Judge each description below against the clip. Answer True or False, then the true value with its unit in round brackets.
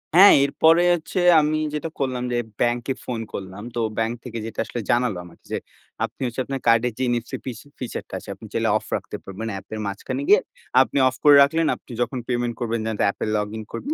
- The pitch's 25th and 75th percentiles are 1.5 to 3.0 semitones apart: False (3.8 semitones)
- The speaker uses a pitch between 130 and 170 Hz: False (120 Hz)